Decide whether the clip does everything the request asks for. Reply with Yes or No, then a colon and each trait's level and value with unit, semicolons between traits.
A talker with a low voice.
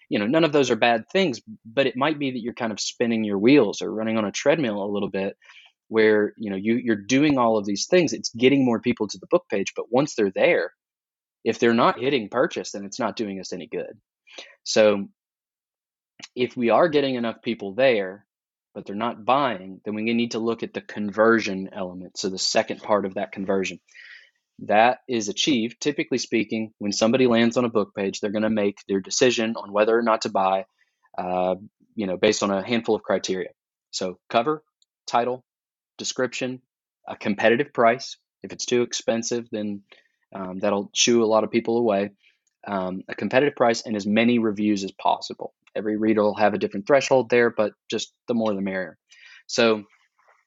Yes: low, 110 Hz